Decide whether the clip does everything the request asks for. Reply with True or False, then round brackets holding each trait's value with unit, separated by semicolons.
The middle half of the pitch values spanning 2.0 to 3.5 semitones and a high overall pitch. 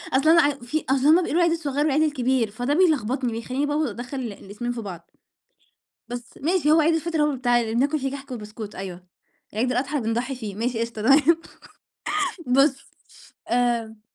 False (4.2 semitones; 255 Hz)